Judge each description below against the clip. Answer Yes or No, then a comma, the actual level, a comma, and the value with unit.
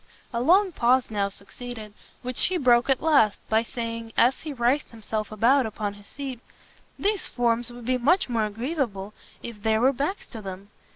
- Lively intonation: No, average, 3.5 semitones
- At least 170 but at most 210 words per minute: Yes, average, 180 wpm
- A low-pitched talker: No, high, 240 Hz